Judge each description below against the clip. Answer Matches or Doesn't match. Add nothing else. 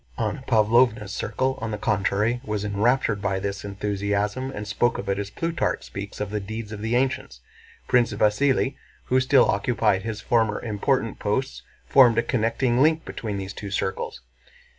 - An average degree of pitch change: Matches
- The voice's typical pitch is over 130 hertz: Doesn't match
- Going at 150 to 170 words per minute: Matches